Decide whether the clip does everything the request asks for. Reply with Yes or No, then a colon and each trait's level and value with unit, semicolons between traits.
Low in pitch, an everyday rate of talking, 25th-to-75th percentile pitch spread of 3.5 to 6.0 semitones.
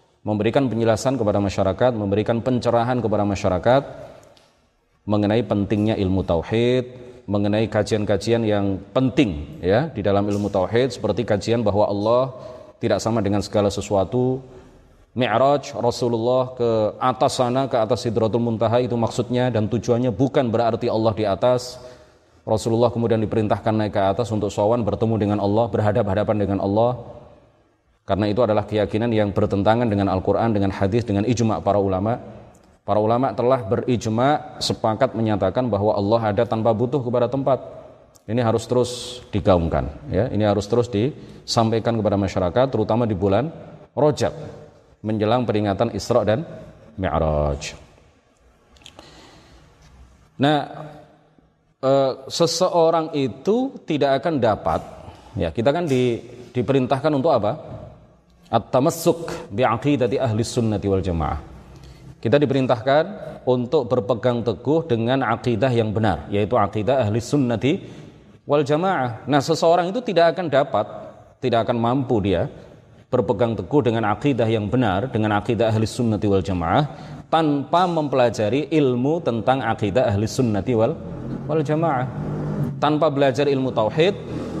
Yes: low, 120 Hz; average, 125 wpm; average, 4.0 semitones